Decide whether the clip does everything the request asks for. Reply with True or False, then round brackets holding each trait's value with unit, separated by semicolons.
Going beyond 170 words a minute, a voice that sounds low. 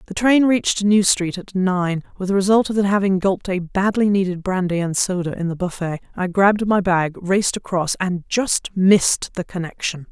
False (190 wpm; 190 Hz)